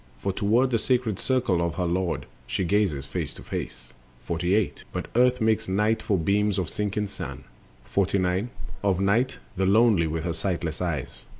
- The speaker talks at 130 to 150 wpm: No, average, 185 wpm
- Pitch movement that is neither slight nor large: Yes, average, 4.0 semitones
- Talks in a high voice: No, very low, 95 Hz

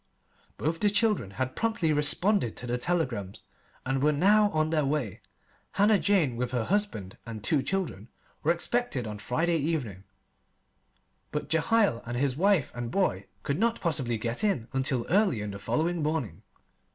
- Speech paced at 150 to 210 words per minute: Yes, average, 165 wpm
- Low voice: No, medium, 150 Hz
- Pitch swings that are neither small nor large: No, wide, 7.7 semitones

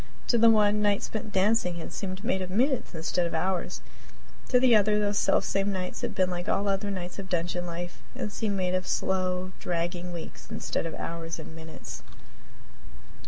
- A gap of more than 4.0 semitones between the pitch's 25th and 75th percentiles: No, average, 2.7 semitones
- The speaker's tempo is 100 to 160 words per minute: No, average, 190 wpm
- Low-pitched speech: No, medium, 185 Hz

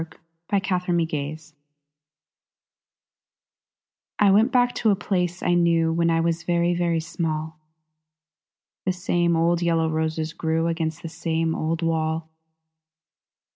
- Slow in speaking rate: Yes, slow, 125 wpm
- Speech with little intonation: Yes, narrow, 1.5 semitones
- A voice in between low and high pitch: Yes, medium, 165 Hz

